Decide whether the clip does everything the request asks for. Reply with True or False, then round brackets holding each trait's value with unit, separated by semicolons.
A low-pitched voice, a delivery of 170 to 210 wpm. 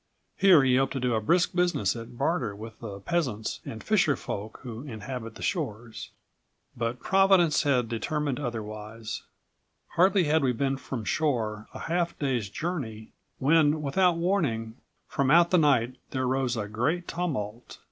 False (130 Hz; 155 wpm)